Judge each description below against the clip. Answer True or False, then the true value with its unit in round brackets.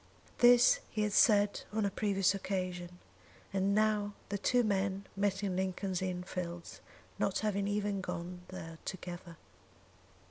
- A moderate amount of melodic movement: False (2.1 semitones)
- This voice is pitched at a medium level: False (195 Hz)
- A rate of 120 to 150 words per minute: True (140 wpm)